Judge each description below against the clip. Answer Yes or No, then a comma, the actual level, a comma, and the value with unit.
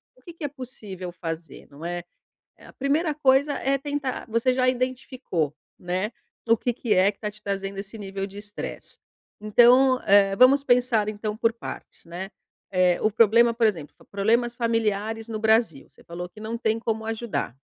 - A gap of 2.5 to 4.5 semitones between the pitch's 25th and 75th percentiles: Yes, average, 4.1 semitones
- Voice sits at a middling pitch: No, high, 220 Hz